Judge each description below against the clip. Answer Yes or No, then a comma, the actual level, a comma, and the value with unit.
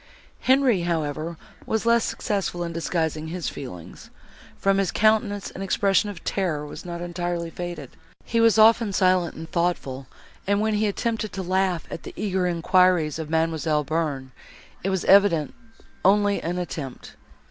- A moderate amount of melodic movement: Yes, average, 3.7 semitones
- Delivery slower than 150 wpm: No, average, 155 wpm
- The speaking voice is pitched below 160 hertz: No, medium, 180 Hz